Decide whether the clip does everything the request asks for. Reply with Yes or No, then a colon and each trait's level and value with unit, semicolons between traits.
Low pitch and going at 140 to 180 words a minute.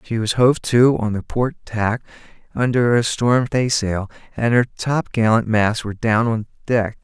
Yes: low, 115 Hz; average, 170 wpm